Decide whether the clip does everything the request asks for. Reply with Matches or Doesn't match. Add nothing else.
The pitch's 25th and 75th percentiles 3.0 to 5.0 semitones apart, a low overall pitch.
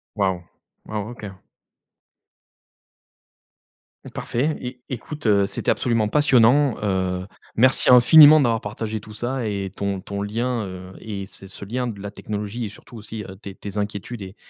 Matches